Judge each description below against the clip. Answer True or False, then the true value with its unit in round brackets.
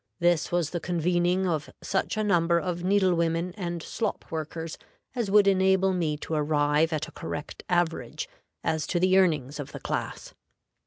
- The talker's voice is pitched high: False (175 Hz)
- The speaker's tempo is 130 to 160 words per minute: False (170 wpm)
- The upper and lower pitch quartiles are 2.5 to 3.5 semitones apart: True (2.8 semitones)